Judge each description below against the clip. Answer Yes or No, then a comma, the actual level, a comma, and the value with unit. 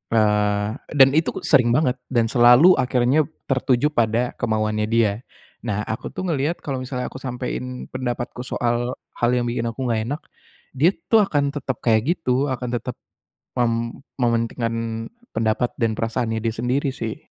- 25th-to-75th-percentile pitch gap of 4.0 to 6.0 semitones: No, narrow, 2.4 semitones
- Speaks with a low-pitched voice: Yes, low, 120 Hz